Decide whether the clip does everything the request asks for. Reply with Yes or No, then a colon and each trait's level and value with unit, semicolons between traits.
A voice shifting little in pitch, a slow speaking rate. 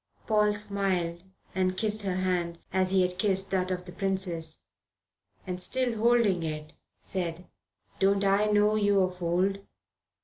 No: narrow, 2.2 semitones; average, 145 wpm